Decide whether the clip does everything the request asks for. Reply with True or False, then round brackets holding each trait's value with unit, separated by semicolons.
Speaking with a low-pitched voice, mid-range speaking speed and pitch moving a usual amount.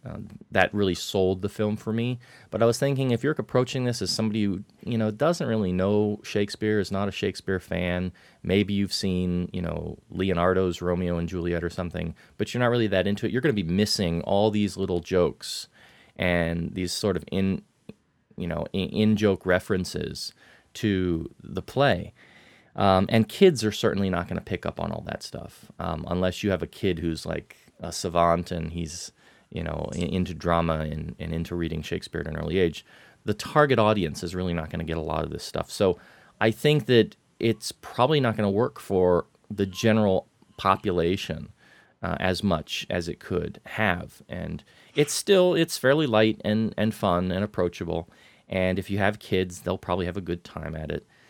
True (95 Hz; 195 wpm; 3.5 semitones)